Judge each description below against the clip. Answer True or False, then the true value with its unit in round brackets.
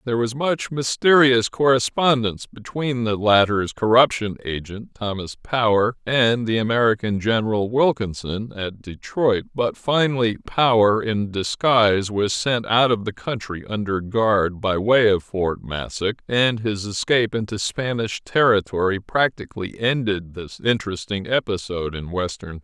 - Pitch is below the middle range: True (110 Hz)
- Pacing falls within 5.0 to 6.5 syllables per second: False (4.6 syllables/s)